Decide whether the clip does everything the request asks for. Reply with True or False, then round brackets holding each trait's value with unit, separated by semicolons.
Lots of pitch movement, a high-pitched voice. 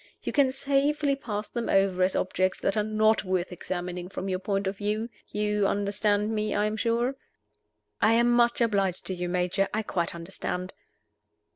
False (3.3 semitones; 205 Hz)